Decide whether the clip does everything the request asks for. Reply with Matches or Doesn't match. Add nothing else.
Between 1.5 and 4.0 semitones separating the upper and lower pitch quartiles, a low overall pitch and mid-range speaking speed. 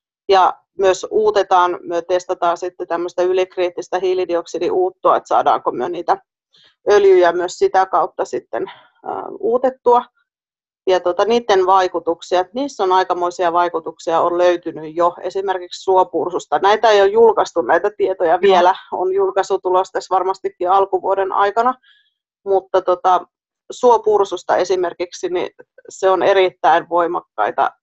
Doesn't match